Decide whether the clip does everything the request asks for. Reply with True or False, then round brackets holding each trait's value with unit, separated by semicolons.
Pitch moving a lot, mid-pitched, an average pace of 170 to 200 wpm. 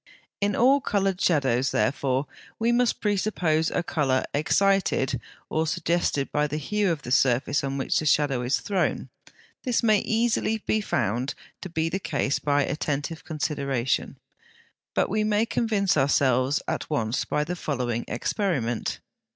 False (6.6 semitones; 155 Hz; 150 wpm)